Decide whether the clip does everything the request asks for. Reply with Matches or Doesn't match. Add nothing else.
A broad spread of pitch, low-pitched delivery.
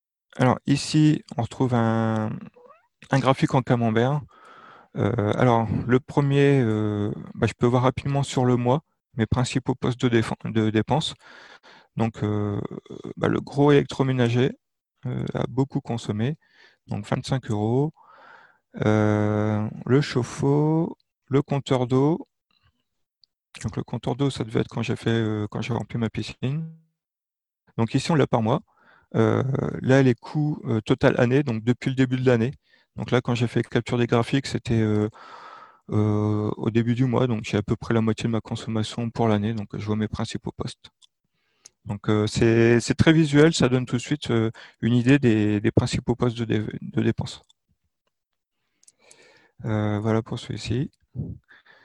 Doesn't match